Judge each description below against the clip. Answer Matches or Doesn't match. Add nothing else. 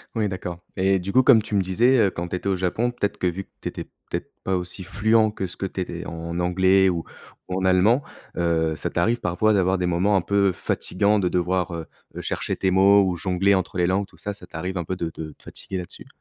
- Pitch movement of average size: Doesn't match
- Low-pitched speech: Matches